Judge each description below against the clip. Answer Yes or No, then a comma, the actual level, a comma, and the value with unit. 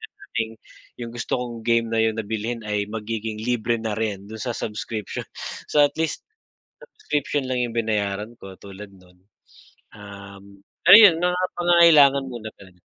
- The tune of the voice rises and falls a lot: No, average, 3.3 semitones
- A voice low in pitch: Yes, low, 110 Hz